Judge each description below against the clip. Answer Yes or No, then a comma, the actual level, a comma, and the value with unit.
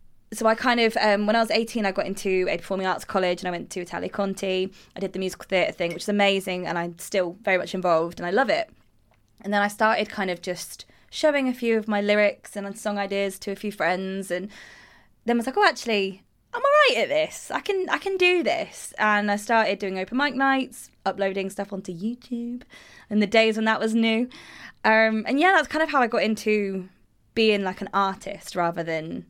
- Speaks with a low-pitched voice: No, high, 205 Hz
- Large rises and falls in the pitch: No, average, 3.4 semitones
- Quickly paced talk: Yes, fast, 230 wpm